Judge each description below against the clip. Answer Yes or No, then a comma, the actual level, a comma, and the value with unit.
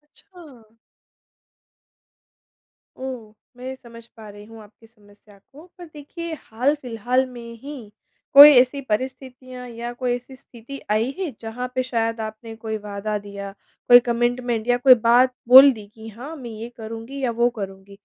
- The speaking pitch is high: Yes, high, 240 Hz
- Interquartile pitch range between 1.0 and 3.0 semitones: Yes, average, 2.7 semitones